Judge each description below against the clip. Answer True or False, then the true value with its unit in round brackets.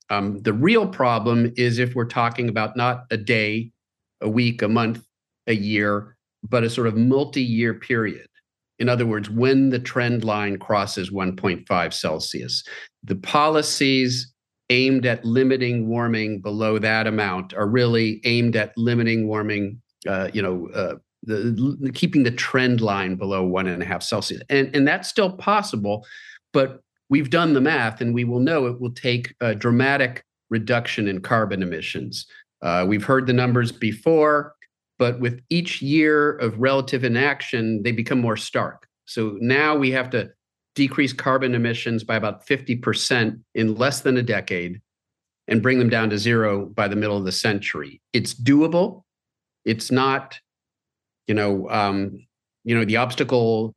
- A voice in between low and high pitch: False (120 Hz)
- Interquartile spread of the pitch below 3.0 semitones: False (3.3 semitones)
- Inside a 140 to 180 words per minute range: True (160 wpm)